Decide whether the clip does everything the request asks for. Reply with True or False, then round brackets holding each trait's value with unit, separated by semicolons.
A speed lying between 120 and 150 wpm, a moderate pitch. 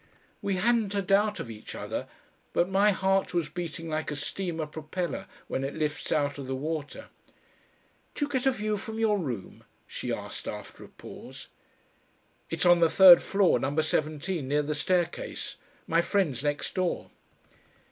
False (165 wpm; 170 Hz)